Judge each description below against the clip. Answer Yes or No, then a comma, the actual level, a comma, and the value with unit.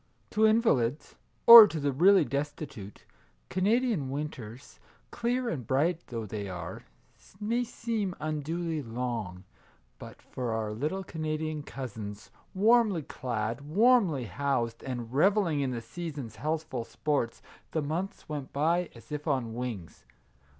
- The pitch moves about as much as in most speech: No, wide, 7.0 semitones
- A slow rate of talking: Yes, slow, 130 wpm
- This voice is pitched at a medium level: Yes, medium, 145 Hz